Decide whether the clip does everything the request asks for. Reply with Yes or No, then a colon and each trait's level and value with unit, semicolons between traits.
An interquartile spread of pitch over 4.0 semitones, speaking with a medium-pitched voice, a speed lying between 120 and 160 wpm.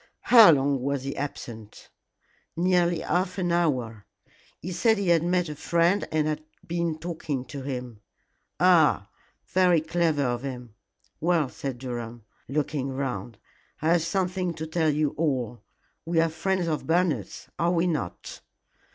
Yes: average, 4.5 semitones; medium, 155 Hz; average, 150 wpm